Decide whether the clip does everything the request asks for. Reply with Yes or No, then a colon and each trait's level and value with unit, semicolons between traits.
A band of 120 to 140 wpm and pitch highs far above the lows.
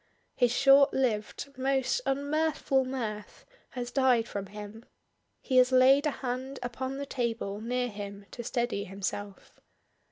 No: slow, 135 wpm; average, 4.1 semitones